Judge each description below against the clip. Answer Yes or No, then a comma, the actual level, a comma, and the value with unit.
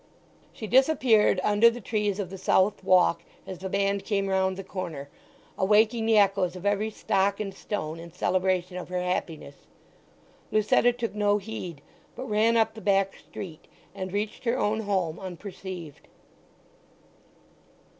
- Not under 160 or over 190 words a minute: No, average, 150 wpm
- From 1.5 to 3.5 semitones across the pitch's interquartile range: Yes, narrow, 2.6 semitones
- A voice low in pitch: No, high, 195 Hz